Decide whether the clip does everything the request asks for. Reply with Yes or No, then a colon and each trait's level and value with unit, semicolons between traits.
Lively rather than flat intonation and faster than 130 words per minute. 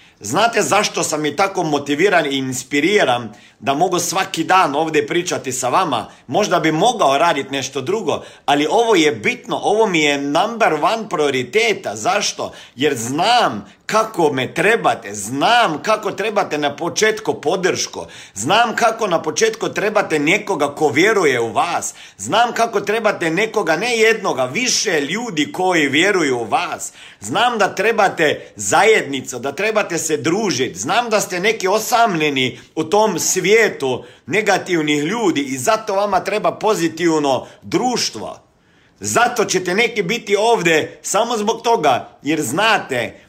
Yes: wide, 6.5 semitones; average, 140 wpm